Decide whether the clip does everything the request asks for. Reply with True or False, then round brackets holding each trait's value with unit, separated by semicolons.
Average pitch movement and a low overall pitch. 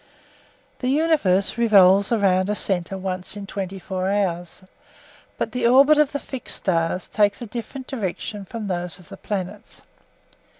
False (4.2 semitones; 200 Hz)